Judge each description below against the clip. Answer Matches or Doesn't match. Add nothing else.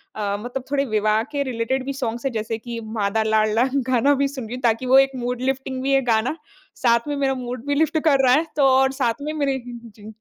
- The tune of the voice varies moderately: Matches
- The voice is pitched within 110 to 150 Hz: Doesn't match